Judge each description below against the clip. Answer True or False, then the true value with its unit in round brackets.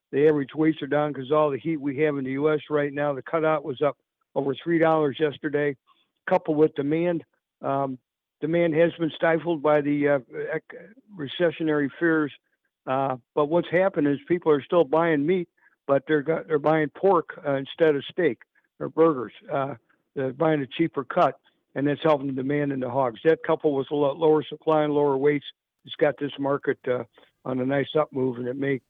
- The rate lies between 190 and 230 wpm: True (200 wpm)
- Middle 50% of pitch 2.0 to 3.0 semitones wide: True (2.5 semitones)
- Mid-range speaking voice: True (150 Hz)